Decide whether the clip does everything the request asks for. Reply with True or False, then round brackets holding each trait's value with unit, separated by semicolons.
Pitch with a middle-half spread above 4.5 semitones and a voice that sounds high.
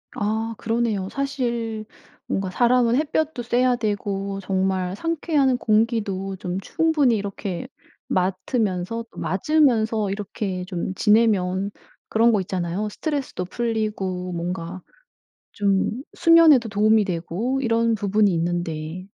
False (4.1 semitones; 210 Hz)